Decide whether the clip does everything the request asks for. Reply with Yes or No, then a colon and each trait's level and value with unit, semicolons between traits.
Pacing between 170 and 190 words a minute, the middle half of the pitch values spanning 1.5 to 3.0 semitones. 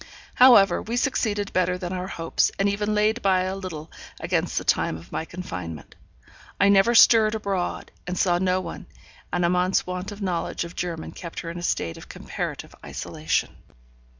Yes: average, 180 wpm; narrow, 2.5 semitones